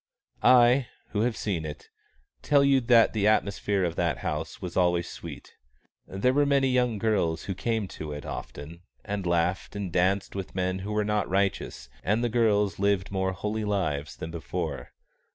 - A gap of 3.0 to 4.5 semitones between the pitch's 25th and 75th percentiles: Yes, average, 4.1 semitones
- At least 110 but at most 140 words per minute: No, average, 175 wpm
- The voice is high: No, low, 100 Hz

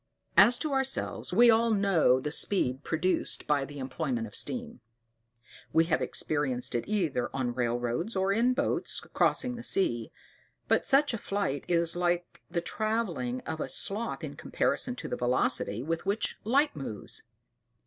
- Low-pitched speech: No, medium, 170 Hz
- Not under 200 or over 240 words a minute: No, average, 160 wpm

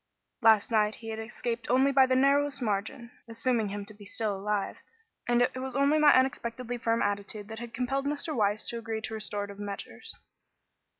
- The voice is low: No, high, 230 Hz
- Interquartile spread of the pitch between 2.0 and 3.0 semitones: No, average, 3.5 semitones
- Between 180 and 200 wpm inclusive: Yes, average, 185 wpm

